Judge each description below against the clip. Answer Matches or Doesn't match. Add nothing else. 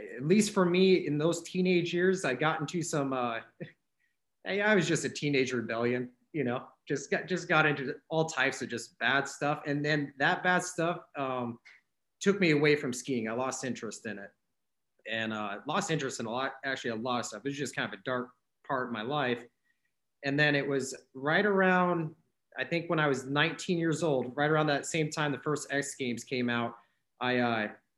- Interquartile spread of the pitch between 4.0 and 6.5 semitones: Matches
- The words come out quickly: Matches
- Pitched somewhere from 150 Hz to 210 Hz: Doesn't match